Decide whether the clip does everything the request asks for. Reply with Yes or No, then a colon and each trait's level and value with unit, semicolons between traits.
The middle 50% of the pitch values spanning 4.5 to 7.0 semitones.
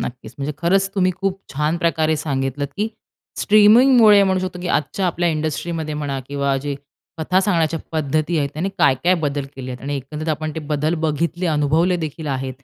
No: average, 3.8 semitones